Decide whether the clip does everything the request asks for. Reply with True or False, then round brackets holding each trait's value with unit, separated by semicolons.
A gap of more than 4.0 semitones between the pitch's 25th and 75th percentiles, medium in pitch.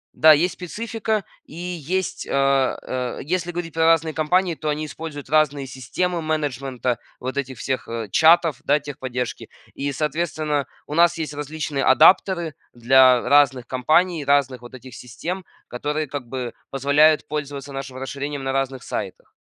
False (3.5 semitones; 145 Hz)